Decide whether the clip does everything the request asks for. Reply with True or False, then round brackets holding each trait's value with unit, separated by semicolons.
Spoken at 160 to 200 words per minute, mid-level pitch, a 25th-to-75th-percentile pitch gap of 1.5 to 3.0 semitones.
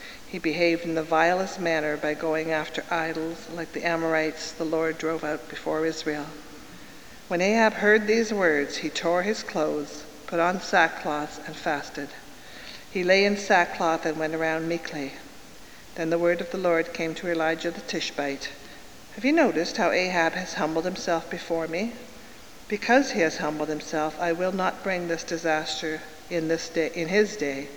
True (170 wpm; 165 Hz; 2.6 semitones)